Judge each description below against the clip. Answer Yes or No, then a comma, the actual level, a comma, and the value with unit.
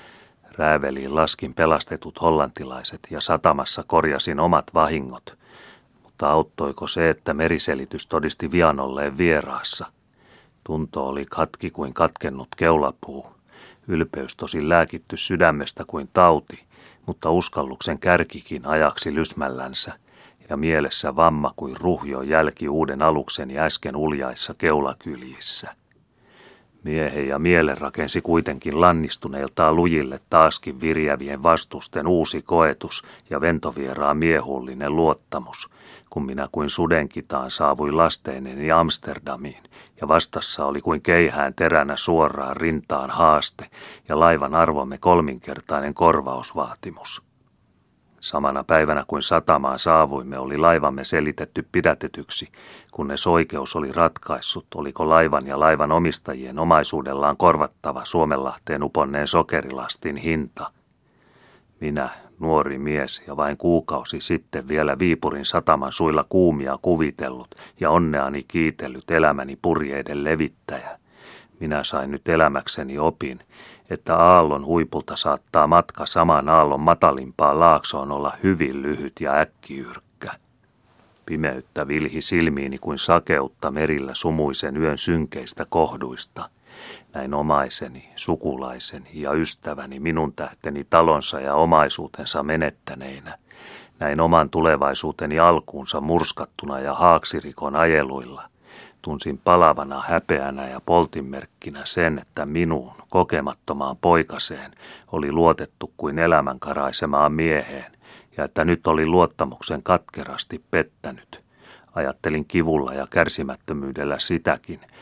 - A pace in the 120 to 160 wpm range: No, average, 105 wpm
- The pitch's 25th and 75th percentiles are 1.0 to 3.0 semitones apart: Yes, average, 2.7 semitones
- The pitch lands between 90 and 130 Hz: No, very low, 75 Hz